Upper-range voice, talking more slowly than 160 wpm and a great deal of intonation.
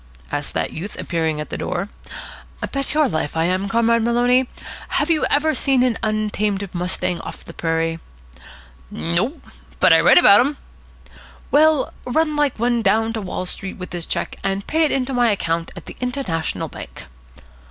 No: high, 220 Hz; average, 175 wpm; wide, 6.5 semitones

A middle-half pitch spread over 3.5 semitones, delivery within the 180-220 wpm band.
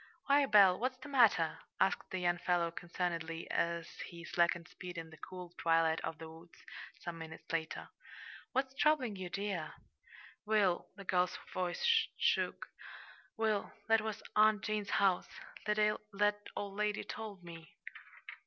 No: average, 3.9 semitones; average, 145 wpm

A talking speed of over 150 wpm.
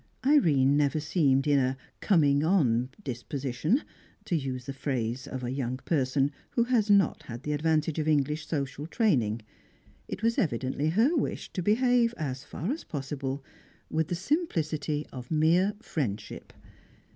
No: average, 145 wpm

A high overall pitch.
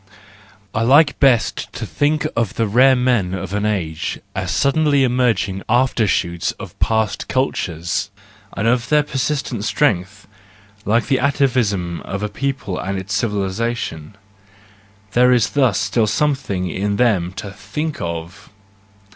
No: low, 110 Hz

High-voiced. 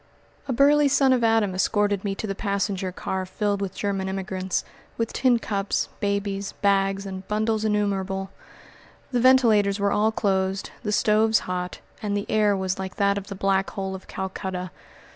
Yes: high, 200 Hz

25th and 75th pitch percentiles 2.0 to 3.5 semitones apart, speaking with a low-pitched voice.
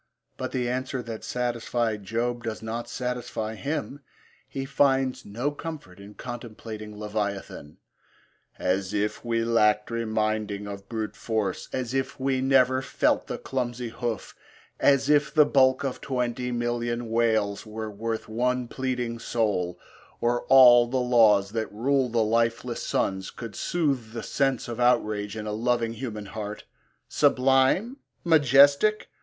Yes: average, 3.1 semitones; low, 120 Hz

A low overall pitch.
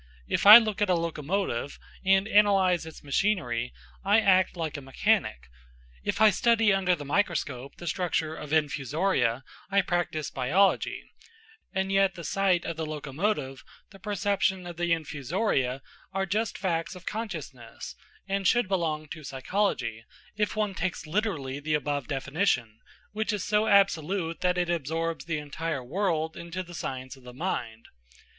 No: medium, 170 Hz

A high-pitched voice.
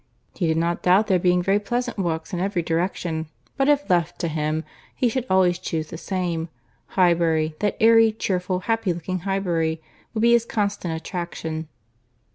No: medium, 180 Hz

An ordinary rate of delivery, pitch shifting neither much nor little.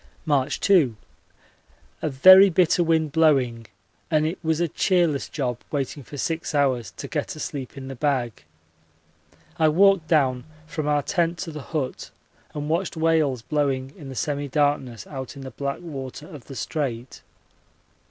Yes: average, 160 wpm; average, 3.4 semitones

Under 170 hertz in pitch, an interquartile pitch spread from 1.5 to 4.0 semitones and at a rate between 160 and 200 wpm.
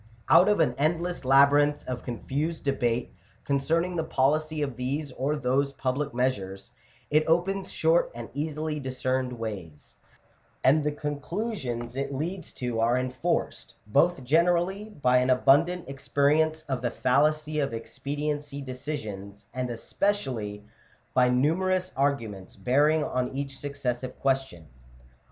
No: medium, 140 Hz; average, 3.6 semitones; slow, 135 wpm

